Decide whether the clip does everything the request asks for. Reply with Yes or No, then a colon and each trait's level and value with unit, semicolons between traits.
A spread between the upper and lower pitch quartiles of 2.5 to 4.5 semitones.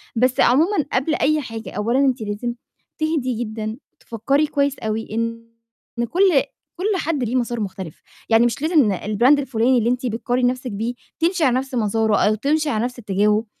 Yes: average, 3.8 semitones